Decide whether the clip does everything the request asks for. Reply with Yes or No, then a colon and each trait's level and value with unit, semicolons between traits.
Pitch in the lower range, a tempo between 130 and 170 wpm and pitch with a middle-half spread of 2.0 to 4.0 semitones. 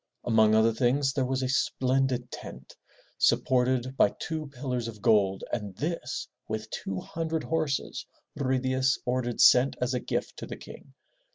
Yes: low, 130 Hz; average, 160 wpm; average, 2.8 semitones